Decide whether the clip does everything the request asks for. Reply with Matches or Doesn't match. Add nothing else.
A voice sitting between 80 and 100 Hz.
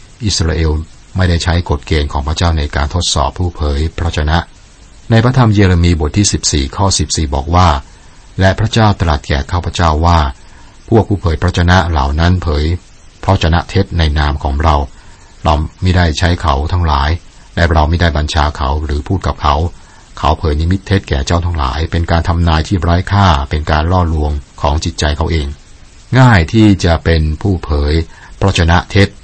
Matches